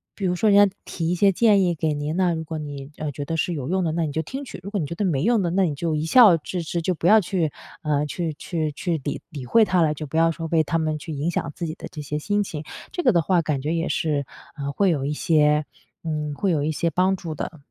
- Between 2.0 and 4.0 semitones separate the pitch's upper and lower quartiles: Yes, average, 3.3 semitones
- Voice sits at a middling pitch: Yes, medium, 165 Hz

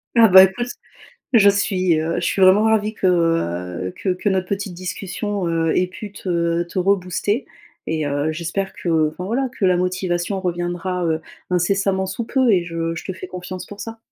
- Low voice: No, medium, 185 Hz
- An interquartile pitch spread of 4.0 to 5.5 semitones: No, average, 2.7 semitones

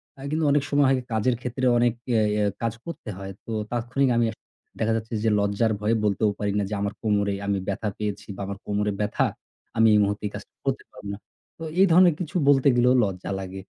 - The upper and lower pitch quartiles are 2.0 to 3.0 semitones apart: No, average, 3.7 semitones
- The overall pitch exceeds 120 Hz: No, low, 110 Hz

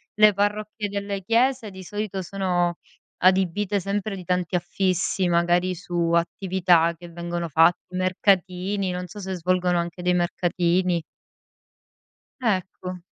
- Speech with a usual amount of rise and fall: No, narrow, 2.2 semitones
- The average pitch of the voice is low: No, medium, 185 Hz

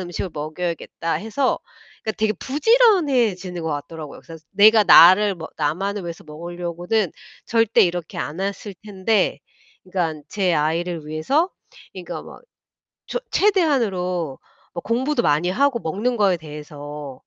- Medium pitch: Yes, medium, 180 Hz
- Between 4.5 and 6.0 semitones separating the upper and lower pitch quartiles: Yes, wide, 5.4 semitones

